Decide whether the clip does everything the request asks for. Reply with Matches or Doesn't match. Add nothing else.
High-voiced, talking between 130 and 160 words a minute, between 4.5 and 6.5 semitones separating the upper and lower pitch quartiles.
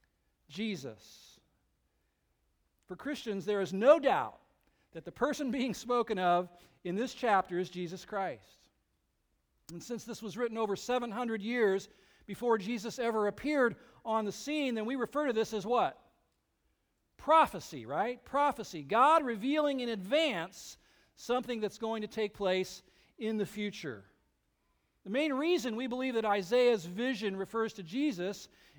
Matches